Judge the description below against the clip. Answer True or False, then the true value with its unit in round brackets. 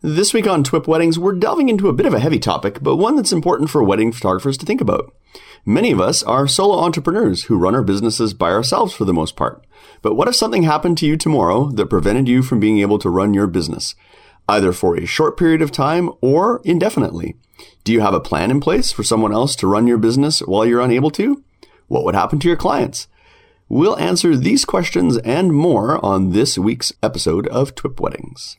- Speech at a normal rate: False (220 wpm)